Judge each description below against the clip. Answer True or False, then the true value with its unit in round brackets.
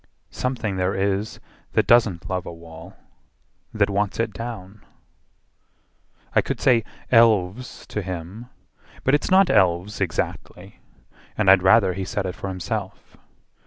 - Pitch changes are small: False (3.7 semitones)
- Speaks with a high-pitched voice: False (100 Hz)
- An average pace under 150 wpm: True (135 wpm)